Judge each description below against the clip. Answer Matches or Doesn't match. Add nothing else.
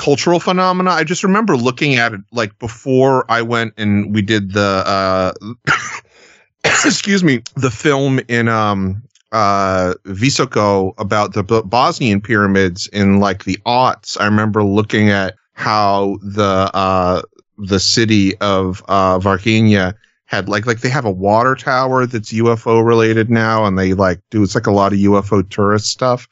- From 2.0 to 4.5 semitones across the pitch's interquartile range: Matches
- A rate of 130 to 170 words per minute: Matches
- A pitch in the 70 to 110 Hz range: Matches